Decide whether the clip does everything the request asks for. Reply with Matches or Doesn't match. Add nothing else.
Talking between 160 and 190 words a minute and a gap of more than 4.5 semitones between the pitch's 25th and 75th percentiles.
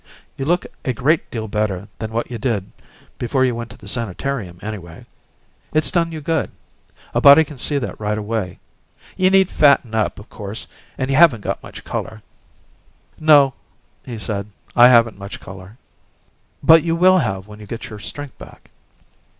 Matches